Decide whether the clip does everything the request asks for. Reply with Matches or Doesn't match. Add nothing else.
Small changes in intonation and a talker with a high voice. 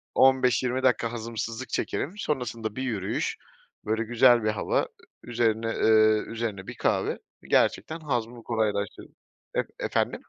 Doesn't match